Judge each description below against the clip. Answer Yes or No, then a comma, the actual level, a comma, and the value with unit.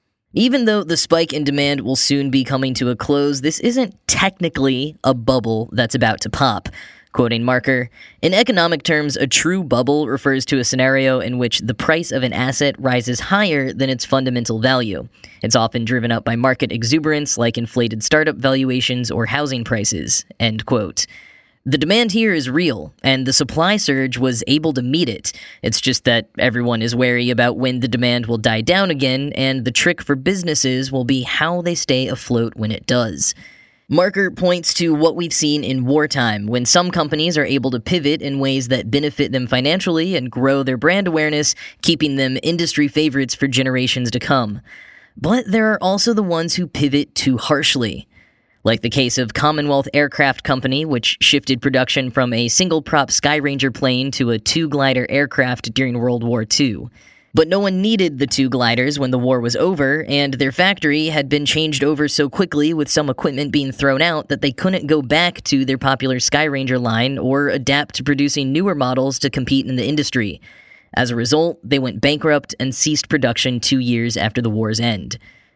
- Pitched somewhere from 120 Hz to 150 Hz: Yes, low, 135 Hz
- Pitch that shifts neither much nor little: Yes, average, 3.3 semitones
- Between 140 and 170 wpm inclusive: No, average, 185 wpm